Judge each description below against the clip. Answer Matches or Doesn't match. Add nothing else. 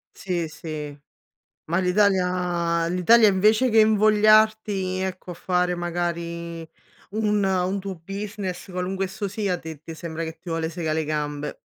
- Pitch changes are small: Doesn't match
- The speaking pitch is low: Doesn't match